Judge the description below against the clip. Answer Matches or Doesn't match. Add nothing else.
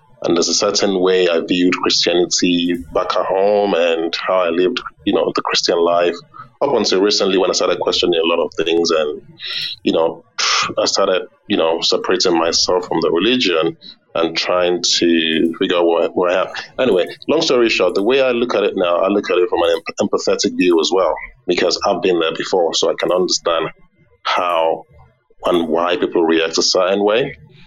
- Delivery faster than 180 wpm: Matches